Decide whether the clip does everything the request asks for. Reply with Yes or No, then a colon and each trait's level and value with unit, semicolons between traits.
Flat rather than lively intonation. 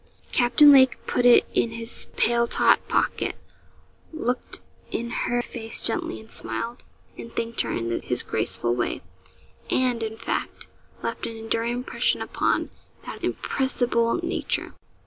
Yes: narrow, 1.5 semitones